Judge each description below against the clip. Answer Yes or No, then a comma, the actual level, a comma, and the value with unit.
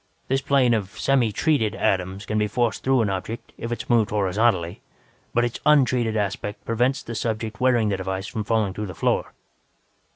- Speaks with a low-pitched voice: Yes, low, 110 Hz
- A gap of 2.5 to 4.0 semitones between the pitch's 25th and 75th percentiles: Yes, average, 3.0 semitones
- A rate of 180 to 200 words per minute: Yes, average, 190 wpm